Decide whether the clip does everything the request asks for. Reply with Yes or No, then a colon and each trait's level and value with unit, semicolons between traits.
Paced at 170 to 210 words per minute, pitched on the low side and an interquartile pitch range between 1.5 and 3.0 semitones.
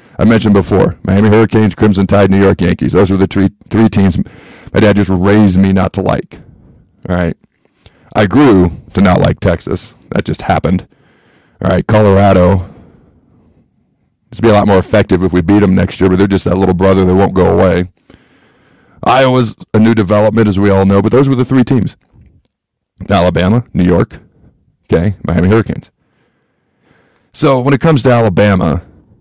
Yes: average, 175 wpm; low, 100 Hz; narrow, 2.5 semitones